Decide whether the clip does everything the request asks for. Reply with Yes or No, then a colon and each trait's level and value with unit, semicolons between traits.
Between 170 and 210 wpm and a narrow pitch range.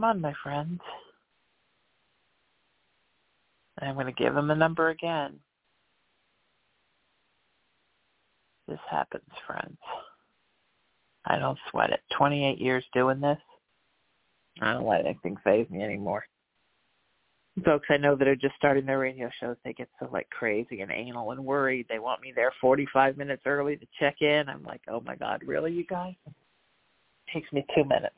No: average, 160 wpm; narrow, 2.0 semitones